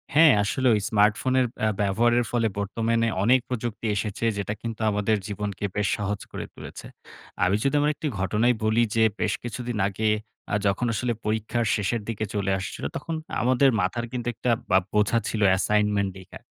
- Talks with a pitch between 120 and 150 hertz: No, low, 110 Hz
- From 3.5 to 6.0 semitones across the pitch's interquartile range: No, average, 2.8 semitones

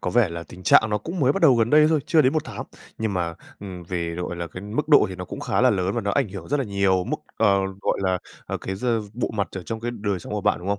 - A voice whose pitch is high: No, low, 100 Hz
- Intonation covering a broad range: No, average, 4.9 semitones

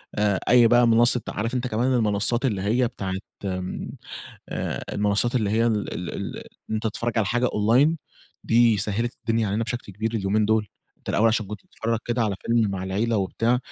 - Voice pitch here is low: Yes, low, 110 Hz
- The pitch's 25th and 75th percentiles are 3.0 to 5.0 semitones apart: No, narrow, 2.4 semitones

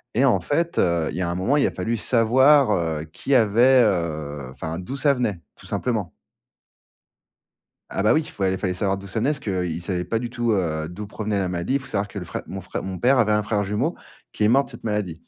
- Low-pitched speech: Yes, low, 105 Hz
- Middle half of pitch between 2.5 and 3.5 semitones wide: No, wide, 5.4 semitones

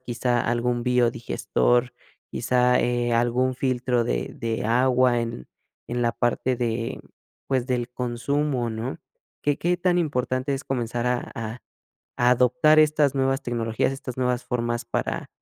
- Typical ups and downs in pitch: No, narrow, 1.5 semitones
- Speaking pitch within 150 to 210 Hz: No, low, 125 Hz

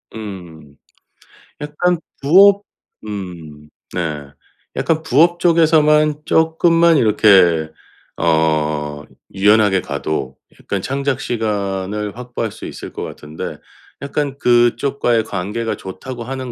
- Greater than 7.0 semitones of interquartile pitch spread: Yes, wide, 8.2 semitones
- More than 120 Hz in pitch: No, low, 110 Hz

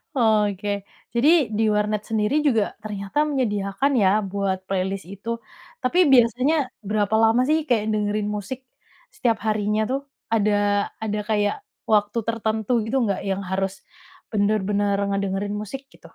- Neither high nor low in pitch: No, high, 210 Hz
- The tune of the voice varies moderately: No, narrow, 2.1 semitones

